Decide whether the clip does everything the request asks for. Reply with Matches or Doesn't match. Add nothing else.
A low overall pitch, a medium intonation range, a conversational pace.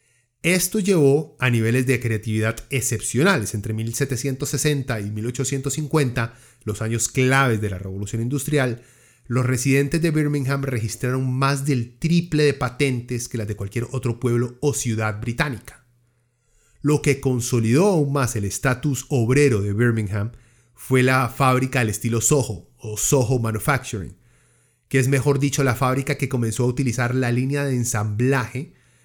Matches